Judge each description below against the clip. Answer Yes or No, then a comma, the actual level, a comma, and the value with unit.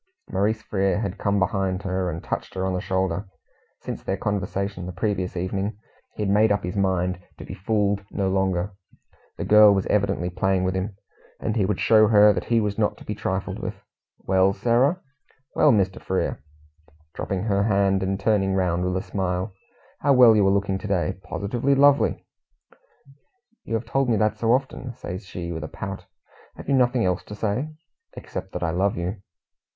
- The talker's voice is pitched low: Yes, low, 100 Hz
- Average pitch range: No, narrow, 2.3 semitones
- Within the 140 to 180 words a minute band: No, average, 190 wpm